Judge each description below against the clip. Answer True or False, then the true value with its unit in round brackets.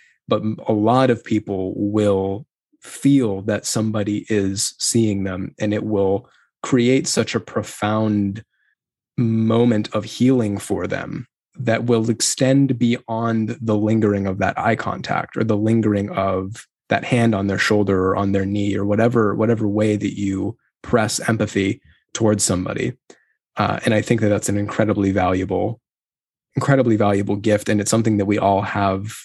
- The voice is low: True (105 Hz)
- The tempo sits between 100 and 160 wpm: True (155 wpm)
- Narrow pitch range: True (2.3 semitones)